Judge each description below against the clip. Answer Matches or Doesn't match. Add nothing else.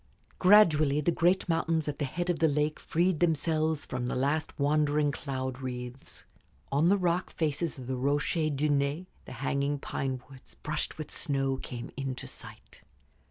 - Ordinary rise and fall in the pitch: Matches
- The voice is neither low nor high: Matches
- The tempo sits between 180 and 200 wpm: Doesn't match